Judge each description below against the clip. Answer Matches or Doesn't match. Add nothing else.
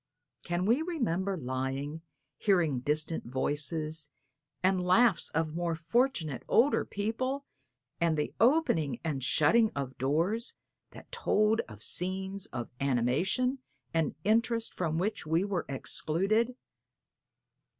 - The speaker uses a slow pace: Matches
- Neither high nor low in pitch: Matches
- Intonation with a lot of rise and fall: Matches